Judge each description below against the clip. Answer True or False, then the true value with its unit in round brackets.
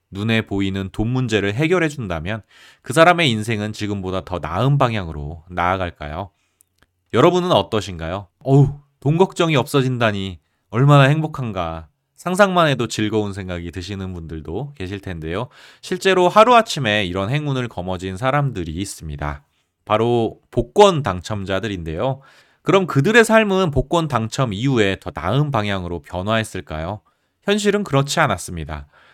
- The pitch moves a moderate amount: False (7.2 semitones)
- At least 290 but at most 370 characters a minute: True (330 characters per minute)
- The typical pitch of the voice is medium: False (110 Hz)